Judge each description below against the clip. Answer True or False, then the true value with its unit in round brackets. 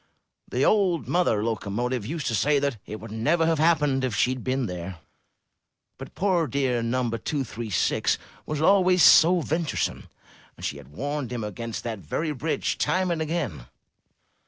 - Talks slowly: False (165 wpm)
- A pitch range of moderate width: False (6.2 semitones)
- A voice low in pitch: True (130 Hz)